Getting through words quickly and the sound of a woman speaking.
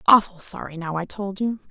Yes: fast, 210 wpm; female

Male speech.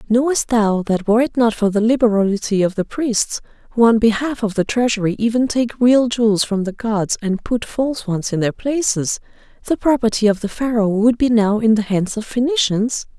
No: female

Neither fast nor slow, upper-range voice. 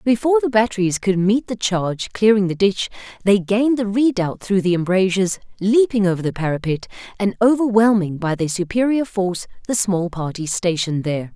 Yes: average, 170 wpm; high, 200 Hz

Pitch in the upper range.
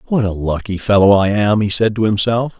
No: low, 105 Hz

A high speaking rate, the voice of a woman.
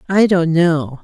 No: average, 175 wpm; female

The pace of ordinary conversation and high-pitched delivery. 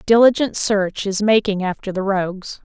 Yes: average, 155 wpm; high, 200 Hz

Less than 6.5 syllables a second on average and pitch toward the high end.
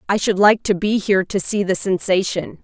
Yes: 5.3 syllables/s; high, 195 Hz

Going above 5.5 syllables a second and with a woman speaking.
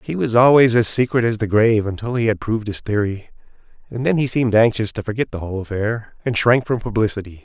No: 6.3 syllables/s; male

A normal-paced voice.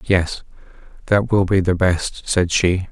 Yes: average, 165 wpm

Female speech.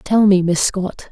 Yes: female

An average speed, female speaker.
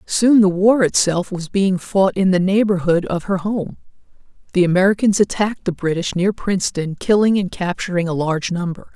Yes: average, 175 wpm; female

